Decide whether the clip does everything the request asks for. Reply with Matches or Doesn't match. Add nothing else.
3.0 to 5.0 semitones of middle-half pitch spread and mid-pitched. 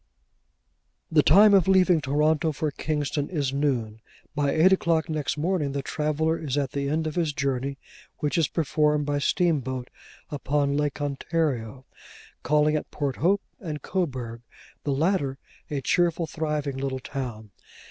Doesn't match